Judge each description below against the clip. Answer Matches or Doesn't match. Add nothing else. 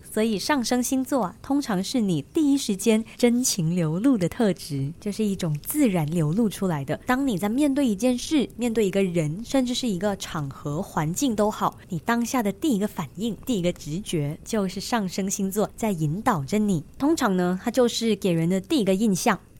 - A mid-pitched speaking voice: Doesn't match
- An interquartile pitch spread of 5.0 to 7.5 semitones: Matches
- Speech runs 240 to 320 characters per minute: Matches